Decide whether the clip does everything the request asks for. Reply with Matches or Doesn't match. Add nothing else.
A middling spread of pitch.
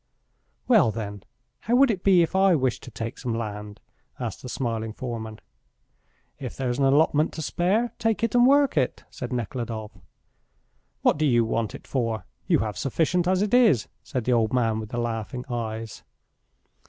Doesn't match